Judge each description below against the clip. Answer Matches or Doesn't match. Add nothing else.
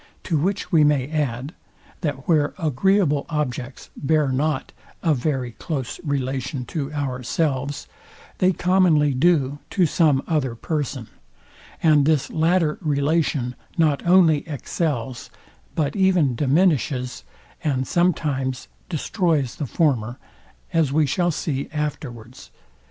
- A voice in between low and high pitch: Matches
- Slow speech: Matches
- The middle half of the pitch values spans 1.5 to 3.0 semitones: Doesn't match